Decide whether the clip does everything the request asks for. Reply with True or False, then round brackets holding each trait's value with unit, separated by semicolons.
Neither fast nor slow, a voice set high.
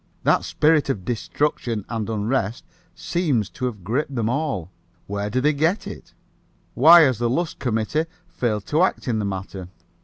False (165 wpm; 120 Hz)